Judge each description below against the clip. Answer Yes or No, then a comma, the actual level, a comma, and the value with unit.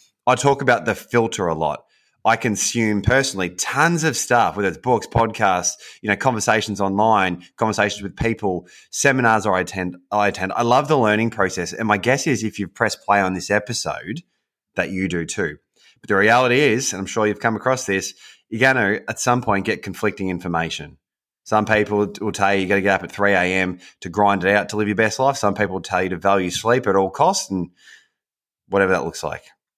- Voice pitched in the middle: No, low, 105 Hz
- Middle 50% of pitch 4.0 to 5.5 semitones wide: No, average, 3.0 semitones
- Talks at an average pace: No, fast, 210 wpm